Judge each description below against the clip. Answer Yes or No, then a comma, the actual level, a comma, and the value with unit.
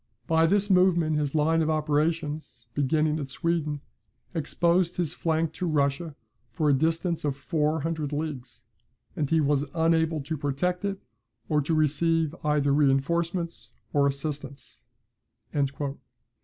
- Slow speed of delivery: Yes, slow, 130 wpm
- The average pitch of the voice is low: No, medium, 155 Hz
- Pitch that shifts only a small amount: Yes, narrow, 2.3 semitones